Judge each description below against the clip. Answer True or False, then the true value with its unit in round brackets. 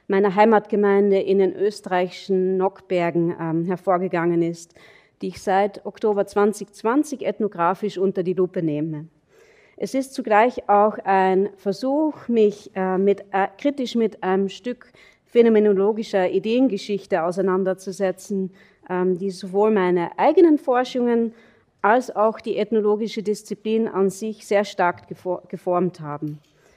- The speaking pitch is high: True (200 Hz)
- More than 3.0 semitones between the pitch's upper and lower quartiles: False (2.7 semitones)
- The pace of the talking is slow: True (120 wpm)